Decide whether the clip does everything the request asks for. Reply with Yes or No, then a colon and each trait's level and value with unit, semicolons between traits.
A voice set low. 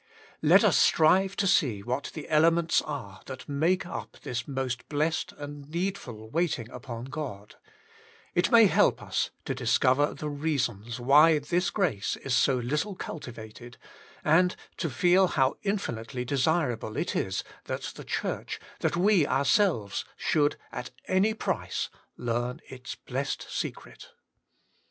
No: medium, 145 Hz